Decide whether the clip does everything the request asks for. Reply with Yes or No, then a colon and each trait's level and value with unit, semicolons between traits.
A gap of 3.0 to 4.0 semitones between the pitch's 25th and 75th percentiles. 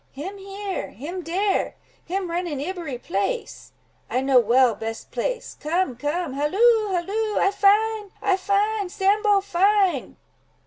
No: wide, 5.6 semitones